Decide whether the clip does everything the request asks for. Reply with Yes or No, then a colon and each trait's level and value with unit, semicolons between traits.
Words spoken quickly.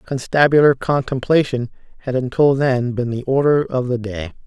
No: average, 150 wpm